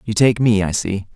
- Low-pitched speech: Yes, low, 105 Hz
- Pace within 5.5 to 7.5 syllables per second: No, 5.0 syllables/s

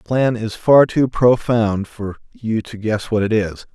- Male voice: Yes, male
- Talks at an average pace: No, fast, 210 wpm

